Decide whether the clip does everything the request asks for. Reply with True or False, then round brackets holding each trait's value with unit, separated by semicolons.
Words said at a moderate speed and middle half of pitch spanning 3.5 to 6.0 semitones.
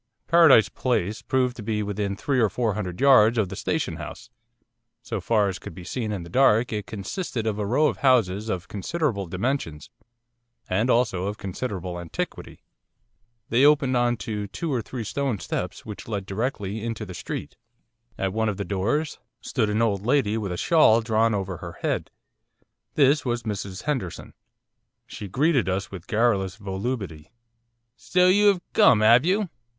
True (175 wpm; 4.6 semitones)